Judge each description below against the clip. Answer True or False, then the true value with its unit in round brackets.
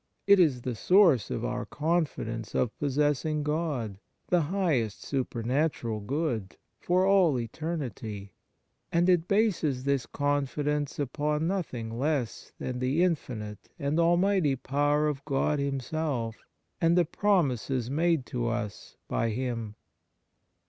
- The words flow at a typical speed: False (120 wpm)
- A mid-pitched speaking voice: True (145 Hz)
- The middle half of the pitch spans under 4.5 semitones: False (5.2 semitones)